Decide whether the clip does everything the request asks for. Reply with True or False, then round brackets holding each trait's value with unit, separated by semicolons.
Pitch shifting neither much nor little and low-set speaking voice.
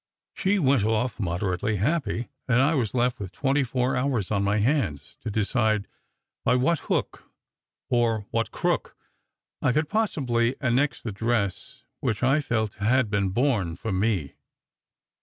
True (4.2 semitones; 115 Hz)